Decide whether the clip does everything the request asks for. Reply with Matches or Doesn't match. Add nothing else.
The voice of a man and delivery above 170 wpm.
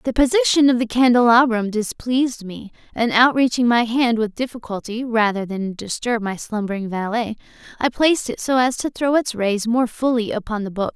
Doesn't match